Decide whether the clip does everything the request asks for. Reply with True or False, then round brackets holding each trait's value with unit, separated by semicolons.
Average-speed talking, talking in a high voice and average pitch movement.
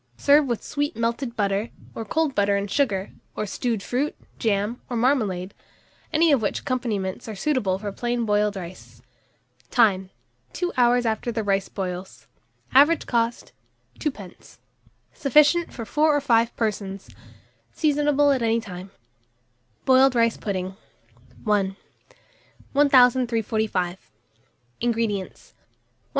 False (125 wpm; 230 Hz; 4.7 semitones)